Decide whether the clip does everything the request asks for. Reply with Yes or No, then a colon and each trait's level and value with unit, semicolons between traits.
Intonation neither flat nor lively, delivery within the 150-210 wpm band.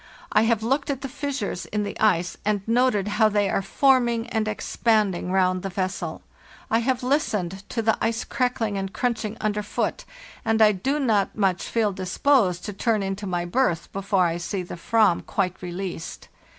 Yes: average, 3.4 semitones; average, 175 wpm